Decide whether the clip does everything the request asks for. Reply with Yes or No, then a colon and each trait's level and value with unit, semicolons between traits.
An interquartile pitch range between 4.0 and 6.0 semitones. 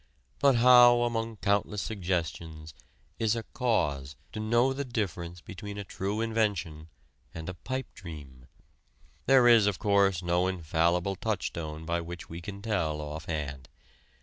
Yes: wide, 5.5 semitones